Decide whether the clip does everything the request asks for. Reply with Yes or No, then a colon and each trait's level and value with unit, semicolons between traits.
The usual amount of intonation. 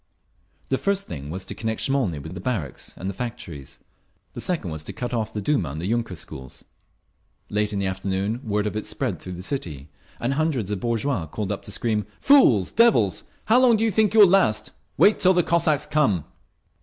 No: wide, 8.0 semitones